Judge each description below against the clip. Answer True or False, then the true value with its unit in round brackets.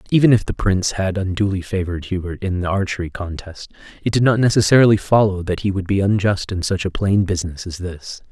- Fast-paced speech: True (210 wpm)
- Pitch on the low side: True (95 Hz)